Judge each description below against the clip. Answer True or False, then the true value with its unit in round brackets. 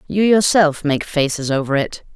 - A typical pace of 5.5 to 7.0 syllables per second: False (4.7 syllables/s)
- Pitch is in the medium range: True (160 Hz)